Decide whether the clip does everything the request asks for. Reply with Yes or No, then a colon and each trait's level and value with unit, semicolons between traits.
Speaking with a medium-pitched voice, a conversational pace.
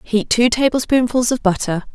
No: high, 235 Hz; average, 155 wpm